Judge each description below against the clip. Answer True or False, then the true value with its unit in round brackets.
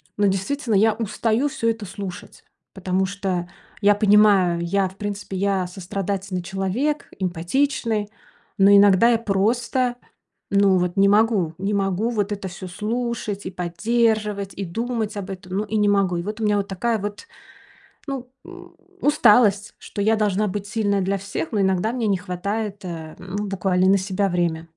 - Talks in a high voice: True (200 Hz)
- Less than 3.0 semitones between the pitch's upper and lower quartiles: True (2.6 semitones)